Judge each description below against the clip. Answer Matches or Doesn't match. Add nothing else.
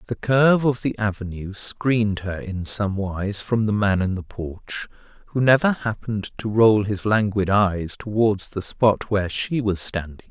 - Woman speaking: Doesn't match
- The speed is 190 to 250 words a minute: Doesn't match